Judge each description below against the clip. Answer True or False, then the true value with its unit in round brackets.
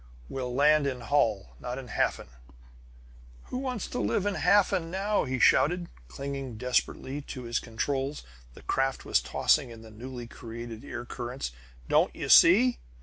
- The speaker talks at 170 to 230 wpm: False (155 wpm)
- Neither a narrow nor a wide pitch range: True (4.3 semitones)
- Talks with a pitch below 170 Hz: True (135 Hz)